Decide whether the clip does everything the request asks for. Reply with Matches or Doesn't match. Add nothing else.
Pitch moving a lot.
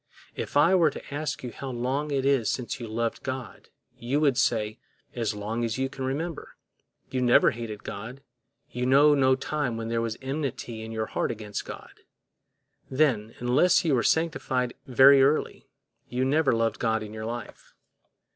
Doesn't match